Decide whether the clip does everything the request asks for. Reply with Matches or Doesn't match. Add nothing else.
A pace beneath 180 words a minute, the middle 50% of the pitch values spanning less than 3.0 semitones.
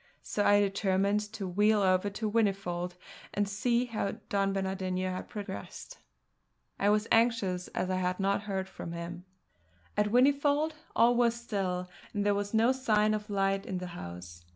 Matches